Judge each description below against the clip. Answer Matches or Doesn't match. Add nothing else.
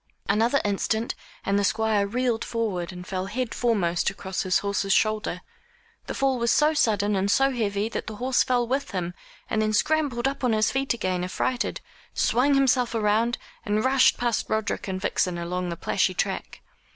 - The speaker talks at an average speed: Matches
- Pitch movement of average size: Matches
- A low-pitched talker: Doesn't match